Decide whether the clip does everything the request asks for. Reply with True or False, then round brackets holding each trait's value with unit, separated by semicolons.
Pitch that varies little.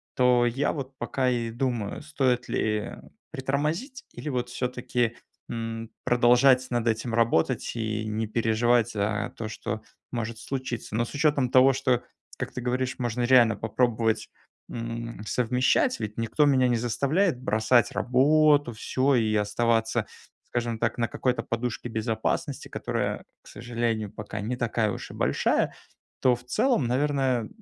True (2.3 semitones)